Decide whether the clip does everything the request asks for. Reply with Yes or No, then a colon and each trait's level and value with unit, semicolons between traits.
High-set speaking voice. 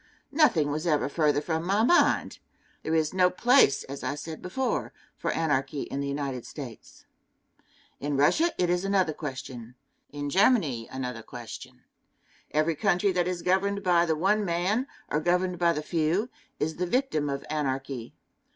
No: medium, 160 Hz